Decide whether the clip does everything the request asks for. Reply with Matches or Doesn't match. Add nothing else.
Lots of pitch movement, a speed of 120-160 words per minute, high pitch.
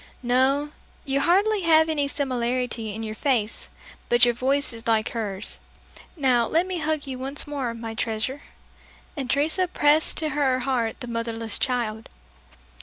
Doesn't match